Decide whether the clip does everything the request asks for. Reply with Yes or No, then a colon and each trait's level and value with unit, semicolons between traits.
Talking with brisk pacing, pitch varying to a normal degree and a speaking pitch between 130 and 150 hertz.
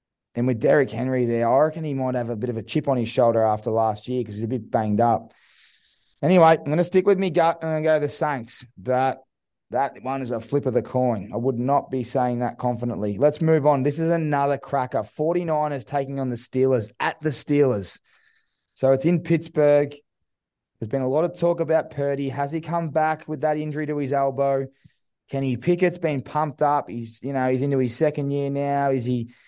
Yes: fast, 230 wpm; average, 3.8 semitones; medium, 140 Hz